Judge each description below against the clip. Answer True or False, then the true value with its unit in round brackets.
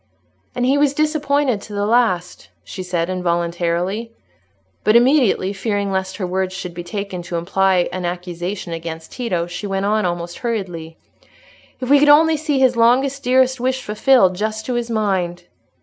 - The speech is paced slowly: False (165 wpm)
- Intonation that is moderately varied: False (5.8 semitones)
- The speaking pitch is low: False (200 Hz)